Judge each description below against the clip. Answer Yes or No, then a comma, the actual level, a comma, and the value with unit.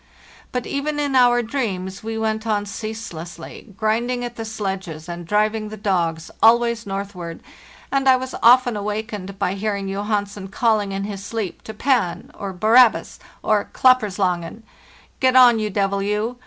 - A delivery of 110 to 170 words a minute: Yes, average, 165 wpm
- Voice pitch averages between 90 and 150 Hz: No, high, 215 Hz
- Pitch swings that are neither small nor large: Yes, average, 3.1 semitones